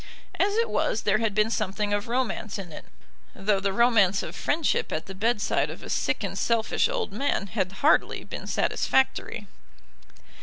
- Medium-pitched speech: No, high, 215 Hz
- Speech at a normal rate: Yes, average, 175 wpm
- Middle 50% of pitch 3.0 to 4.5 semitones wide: Yes, average, 3.4 semitones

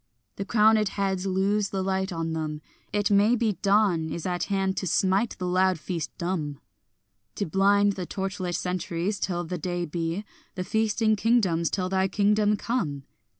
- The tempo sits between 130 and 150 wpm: No, average, 170 wpm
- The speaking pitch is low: No, high, 190 Hz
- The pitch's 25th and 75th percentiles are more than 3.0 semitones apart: No, narrow, 2.6 semitones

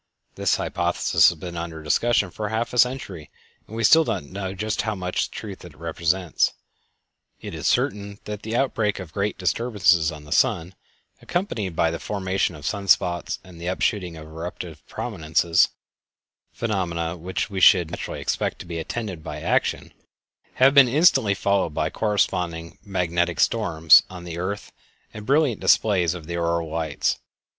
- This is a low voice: Yes, very low, 90 Hz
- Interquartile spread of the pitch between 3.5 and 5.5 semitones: Yes, average, 4.1 semitones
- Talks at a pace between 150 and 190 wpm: Yes, average, 165 wpm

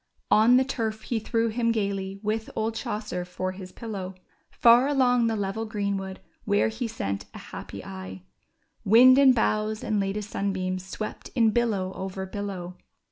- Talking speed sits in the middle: Yes, average, 160 wpm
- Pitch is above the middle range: Yes, high, 210 Hz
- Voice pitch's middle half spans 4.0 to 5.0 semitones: No, average, 3.1 semitones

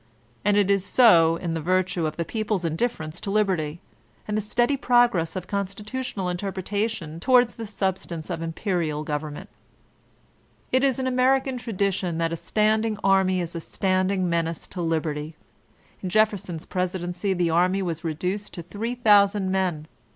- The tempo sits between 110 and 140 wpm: No, average, 150 wpm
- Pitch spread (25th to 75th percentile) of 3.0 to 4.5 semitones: Yes, average, 4.0 semitones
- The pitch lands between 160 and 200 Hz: Yes, medium, 185 Hz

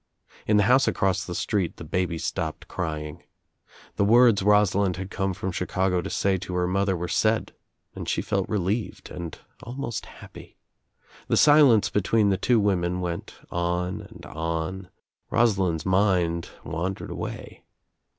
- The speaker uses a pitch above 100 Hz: No, very low, 95 Hz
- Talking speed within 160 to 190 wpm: No, average, 150 wpm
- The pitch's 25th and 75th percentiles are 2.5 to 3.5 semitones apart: Yes, average, 2.9 semitones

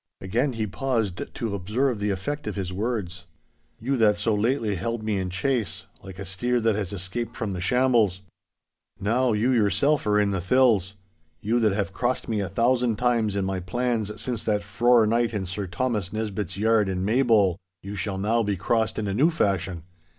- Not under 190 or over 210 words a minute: Yes, average, 195 wpm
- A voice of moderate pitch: No, low, 105 Hz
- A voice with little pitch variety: No, average, 3.5 semitones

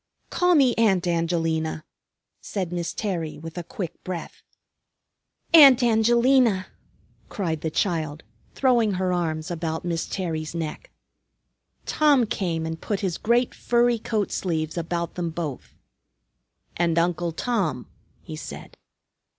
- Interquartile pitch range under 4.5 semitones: No, wide, 5.4 semitones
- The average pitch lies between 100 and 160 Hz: No, medium, 175 Hz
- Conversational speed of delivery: No, slow, 125 wpm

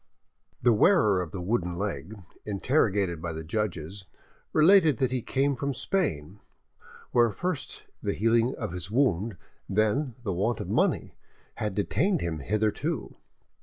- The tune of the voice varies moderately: No, wide, 5.9 semitones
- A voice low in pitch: Yes, low, 110 Hz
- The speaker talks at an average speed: Yes, average, 145 wpm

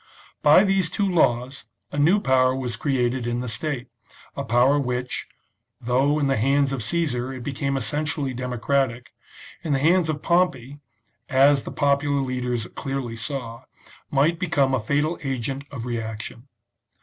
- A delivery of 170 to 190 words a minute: No, average, 150 wpm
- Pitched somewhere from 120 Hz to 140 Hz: Yes, low, 135 Hz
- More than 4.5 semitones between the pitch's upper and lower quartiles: No, average, 2.8 semitones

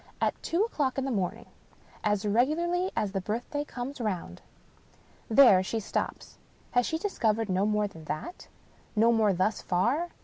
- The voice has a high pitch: Yes, high, 225 Hz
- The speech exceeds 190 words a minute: No, average, 160 wpm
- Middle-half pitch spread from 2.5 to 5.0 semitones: No, wide, 5.6 semitones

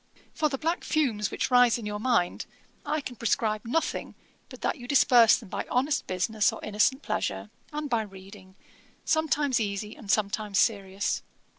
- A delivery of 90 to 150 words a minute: No, average, 165 wpm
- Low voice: No, high, 225 Hz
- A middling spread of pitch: Yes, average, 4.7 semitones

